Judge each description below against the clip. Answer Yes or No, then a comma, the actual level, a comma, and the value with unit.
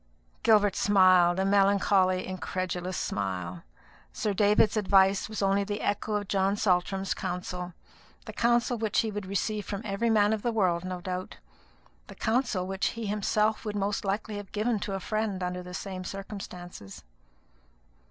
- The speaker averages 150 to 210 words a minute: Yes, average, 160 wpm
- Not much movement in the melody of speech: Yes, narrow, 2.3 semitones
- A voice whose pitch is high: Yes, high, 195 Hz